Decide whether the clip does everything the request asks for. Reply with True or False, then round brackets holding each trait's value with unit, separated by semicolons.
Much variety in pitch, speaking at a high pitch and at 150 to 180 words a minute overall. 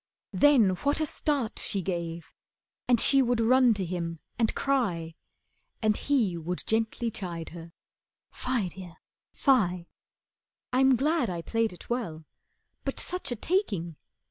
False (6.9 semitones; 220 Hz; 140 wpm)